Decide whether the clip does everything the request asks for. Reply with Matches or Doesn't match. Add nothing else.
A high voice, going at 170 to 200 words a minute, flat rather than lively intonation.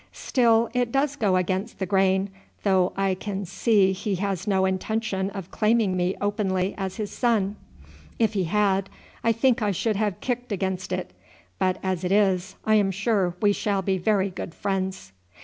Matches